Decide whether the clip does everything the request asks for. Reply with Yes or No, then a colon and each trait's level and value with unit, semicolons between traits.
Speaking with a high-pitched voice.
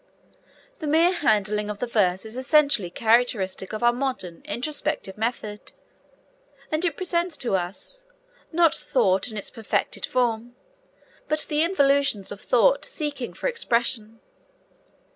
Yes: high, 245 Hz